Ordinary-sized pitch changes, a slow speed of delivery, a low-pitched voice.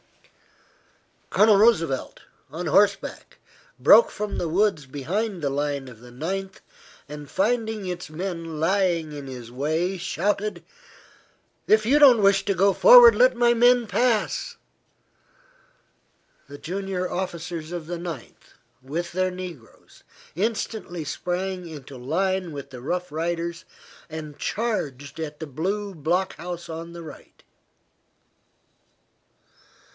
No: average, 4.4 semitones; slow, 120 wpm; medium, 175 Hz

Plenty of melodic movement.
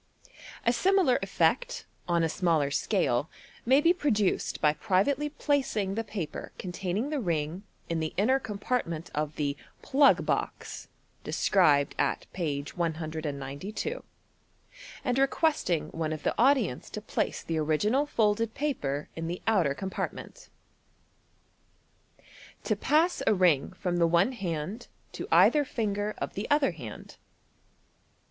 Yes: wide, 8.2 semitones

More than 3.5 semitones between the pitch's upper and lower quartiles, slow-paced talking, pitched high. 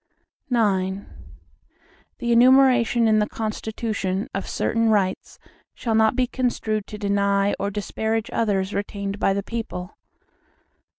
No: narrow, 2.5 semitones; slow, 120 wpm; high, 215 Hz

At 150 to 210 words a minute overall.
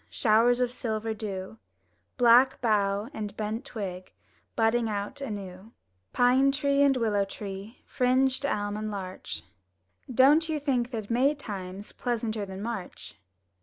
No: slow, 135 wpm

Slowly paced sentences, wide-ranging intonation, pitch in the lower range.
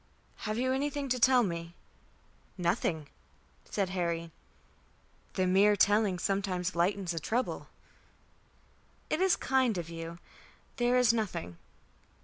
No: slow, 120 wpm; wide, 6.1 semitones; high, 195 Hz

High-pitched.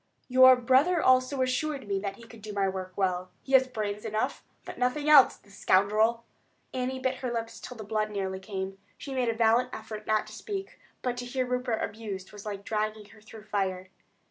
Yes: high, 220 Hz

